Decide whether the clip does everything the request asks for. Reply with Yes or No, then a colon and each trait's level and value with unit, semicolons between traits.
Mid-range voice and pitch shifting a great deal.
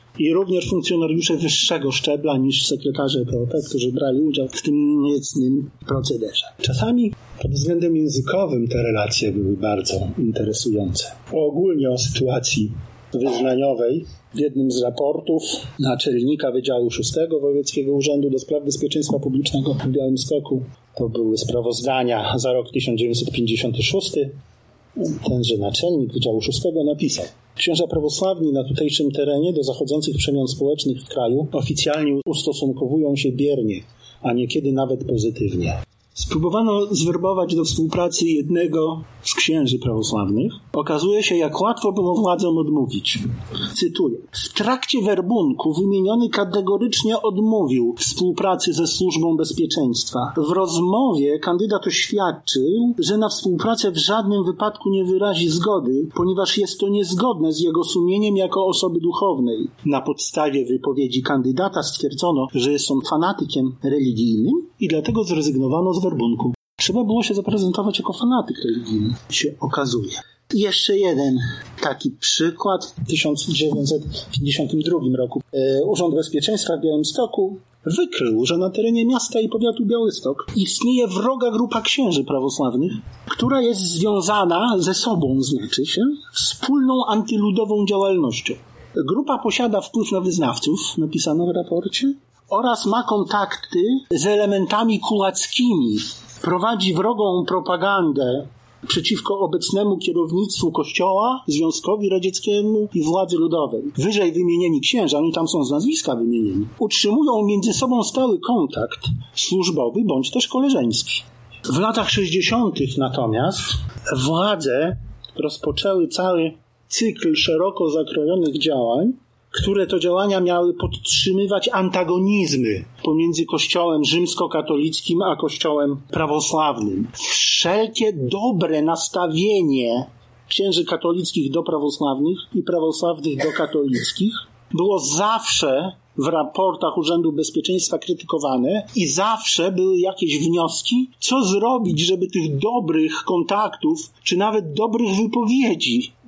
Yes: medium, 170 Hz; wide, 6.6 semitones